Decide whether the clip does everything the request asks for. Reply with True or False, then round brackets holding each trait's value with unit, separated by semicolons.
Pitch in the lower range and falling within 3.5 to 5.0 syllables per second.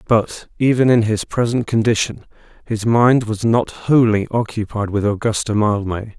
True (110 Hz; 4.6 syllables/s)